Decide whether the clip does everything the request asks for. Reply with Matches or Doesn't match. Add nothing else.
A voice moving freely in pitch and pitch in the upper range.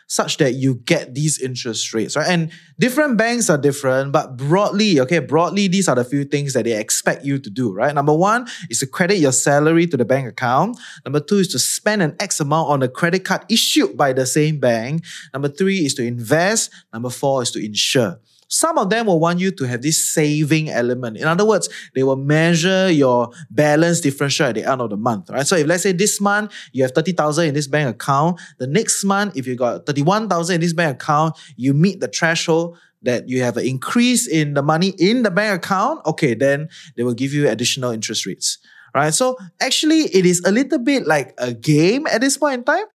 Doesn't match